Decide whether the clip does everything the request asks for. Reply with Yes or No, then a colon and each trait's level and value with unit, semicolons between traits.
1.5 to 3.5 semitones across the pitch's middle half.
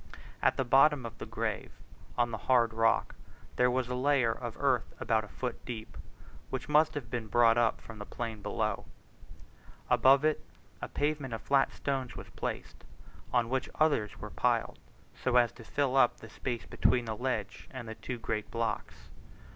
Yes: average, 2.7 semitones